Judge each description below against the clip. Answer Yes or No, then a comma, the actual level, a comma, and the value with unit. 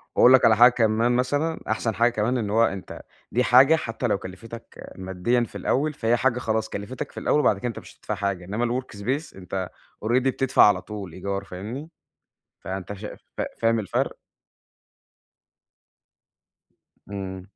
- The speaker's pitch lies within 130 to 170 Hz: No, low, 115 Hz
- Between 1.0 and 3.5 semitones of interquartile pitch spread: No, average, 3.9 semitones